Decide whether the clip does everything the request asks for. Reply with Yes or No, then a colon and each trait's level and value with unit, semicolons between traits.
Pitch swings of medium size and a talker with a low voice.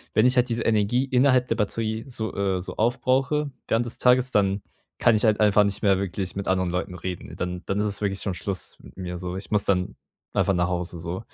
Yes: average, 3.8 semitones; low, 100 Hz